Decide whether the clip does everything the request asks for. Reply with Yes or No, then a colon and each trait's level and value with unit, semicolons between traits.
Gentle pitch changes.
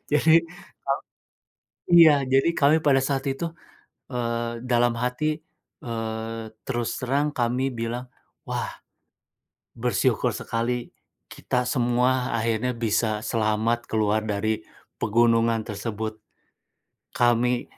Yes: narrow, 2.3 semitones